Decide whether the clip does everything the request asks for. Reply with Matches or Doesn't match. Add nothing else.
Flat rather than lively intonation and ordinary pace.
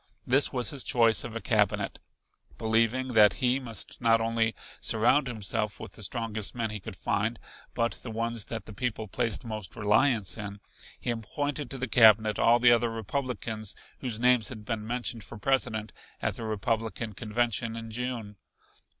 Matches